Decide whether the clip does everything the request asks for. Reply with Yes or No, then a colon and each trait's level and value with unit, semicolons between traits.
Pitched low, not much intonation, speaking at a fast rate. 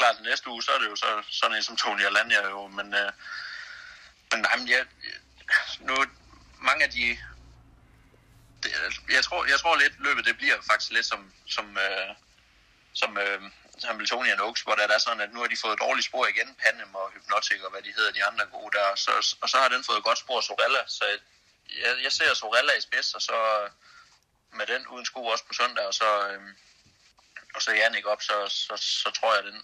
Yes: low, 100 Hz; narrow, 1.6 semitones; fast, 235 wpm